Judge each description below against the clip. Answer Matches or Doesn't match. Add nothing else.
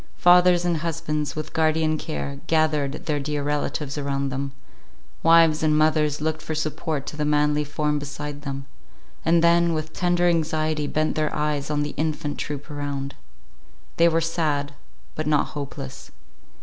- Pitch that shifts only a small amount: Matches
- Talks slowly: Doesn't match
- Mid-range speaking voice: Matches